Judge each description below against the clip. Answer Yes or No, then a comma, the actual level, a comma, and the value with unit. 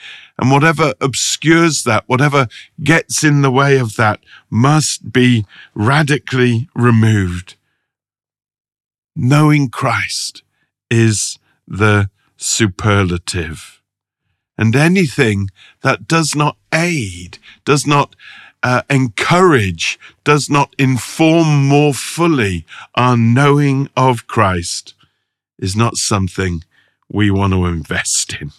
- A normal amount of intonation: No, wide, 5.7 semitones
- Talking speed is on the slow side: Yes, slow, 100 wpm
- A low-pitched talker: Yes, low, 125 Hz